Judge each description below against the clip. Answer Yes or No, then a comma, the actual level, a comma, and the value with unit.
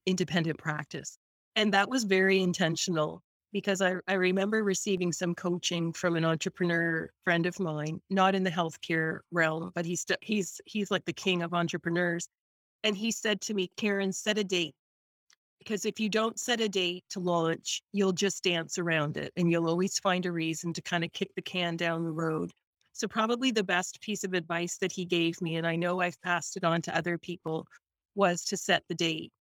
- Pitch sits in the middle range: Yes, medium, 180 Hz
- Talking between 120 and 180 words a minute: No, average, 200 wpm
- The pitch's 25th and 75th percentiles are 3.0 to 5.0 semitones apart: No, narrow, 2.6 semitones